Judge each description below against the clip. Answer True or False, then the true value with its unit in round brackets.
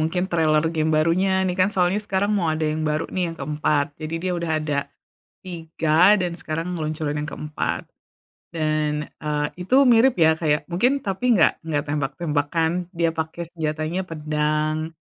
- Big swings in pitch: False (2.6 semitones)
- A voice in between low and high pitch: True (160 Hz)